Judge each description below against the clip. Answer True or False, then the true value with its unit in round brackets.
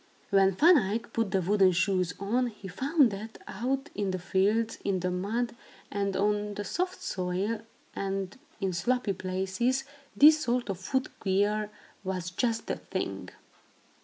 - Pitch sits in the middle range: False (205 Hz)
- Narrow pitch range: False (3.8 semitones)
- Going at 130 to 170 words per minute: True (155 wpm)